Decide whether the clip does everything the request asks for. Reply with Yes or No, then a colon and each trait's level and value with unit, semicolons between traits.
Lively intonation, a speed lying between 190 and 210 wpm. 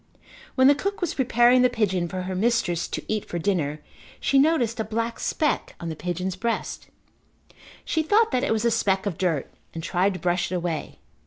Yes: wide, 5.8 semitones; average, 200 wpm